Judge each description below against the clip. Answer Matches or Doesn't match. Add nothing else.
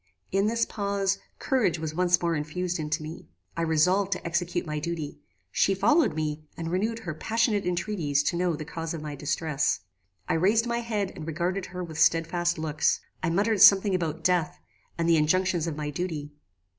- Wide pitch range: Doesn't match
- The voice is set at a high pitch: Doesn't match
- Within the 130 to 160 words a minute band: Doesn't match